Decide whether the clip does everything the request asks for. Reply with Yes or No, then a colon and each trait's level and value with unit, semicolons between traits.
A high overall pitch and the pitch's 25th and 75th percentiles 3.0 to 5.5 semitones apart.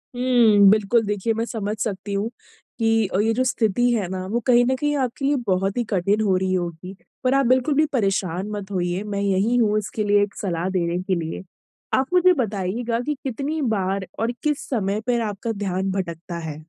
Yes: high, 205 Hz; average, 4.1 semitones